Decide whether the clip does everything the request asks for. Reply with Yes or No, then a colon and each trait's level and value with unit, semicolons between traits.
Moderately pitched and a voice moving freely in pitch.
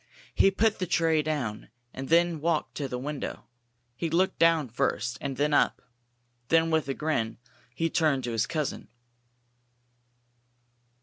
No: medium, 155 Hz; average, 3.5 semitones